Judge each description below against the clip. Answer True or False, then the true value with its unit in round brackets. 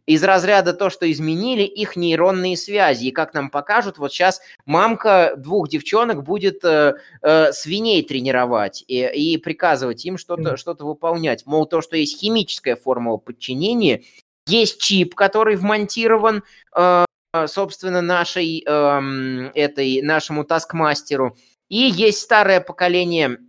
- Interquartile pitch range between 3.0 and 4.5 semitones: False (4.9 semitones)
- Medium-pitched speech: True (170 Hz)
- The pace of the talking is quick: False (130 wpm)